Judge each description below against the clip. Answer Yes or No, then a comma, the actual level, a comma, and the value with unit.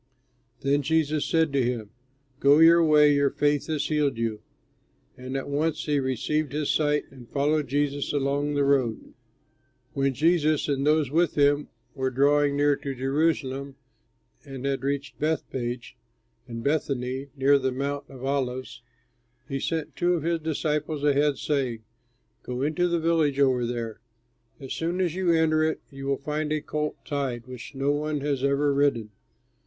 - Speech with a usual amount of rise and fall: No, narrow, 2.2 semitones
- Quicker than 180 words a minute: No, average, 160 wpm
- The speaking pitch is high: No, medium, 145 Hz